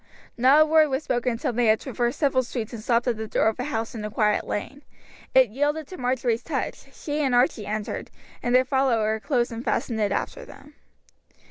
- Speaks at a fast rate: Yes, fast, 215 wpm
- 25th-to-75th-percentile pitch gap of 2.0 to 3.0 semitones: No, average, 3.4 semitones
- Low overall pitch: No, high, 245 Hz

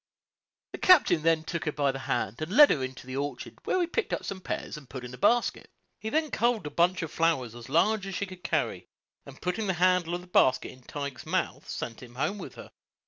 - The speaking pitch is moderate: Yes, medium, 165 Hz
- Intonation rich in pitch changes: Yes, wide, 6.4 semitones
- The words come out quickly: Yes, fast, 245 wpm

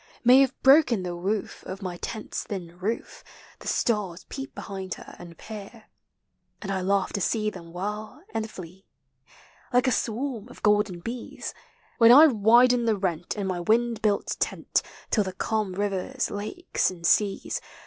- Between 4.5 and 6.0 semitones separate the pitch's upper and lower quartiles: No, average, 3.8 semitones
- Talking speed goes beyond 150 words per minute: Yes, average, 165 wpm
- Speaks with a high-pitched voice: Yes, high, 210 Hz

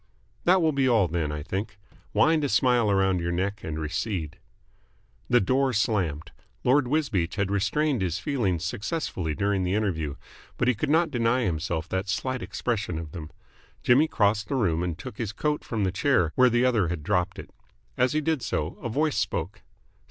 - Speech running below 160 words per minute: No, average, 190 wpm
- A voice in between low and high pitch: No, low, 105 Hz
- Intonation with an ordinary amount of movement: No, wide, 6.4 semitones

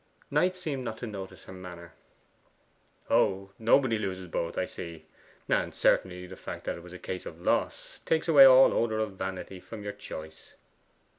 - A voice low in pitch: Yes, very low, 95 Hz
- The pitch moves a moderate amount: Yes, average, 4.1 semitones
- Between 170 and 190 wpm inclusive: Yes, average, 180 wpm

